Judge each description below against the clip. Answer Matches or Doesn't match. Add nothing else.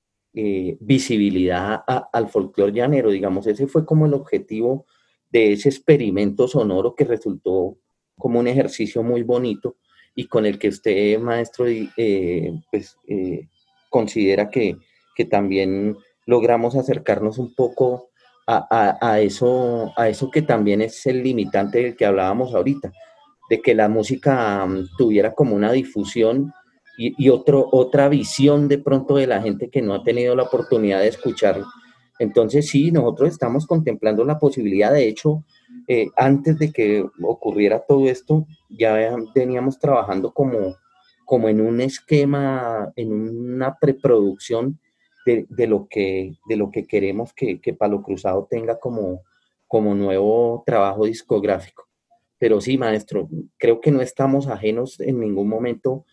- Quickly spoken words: Doesn't match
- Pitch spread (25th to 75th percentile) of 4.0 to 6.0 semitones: Matches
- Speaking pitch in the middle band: Doesn't match